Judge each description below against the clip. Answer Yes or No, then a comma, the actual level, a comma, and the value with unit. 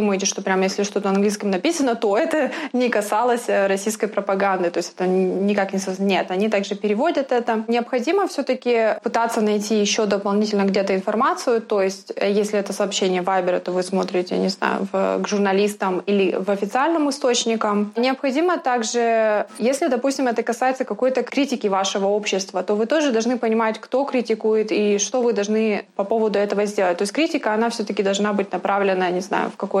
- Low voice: No, high, 210 Hz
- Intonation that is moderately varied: Yes, average, 3.4 semitones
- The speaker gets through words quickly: Yes, fast, 175 wpm